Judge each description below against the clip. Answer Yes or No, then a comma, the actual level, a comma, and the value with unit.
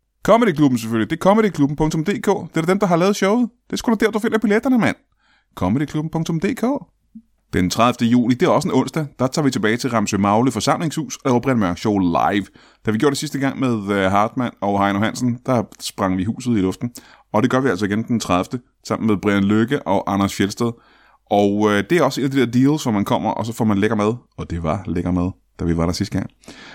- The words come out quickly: Yes, fast, 235 wpm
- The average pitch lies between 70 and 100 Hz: No, low, 120 Hz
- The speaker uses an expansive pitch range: Yes, wide, 7.0 semitones